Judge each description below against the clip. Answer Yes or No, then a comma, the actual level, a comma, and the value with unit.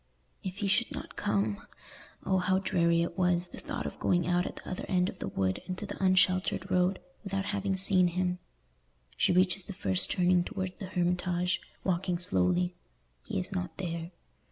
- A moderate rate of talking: Yes, average, 175 wpm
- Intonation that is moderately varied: No, narrow, 1.4 semitones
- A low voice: No, medium, 180 Hz